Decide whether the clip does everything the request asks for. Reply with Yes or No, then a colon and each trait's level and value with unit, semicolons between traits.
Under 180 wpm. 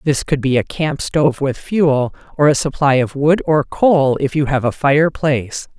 No: fast, 205 wpm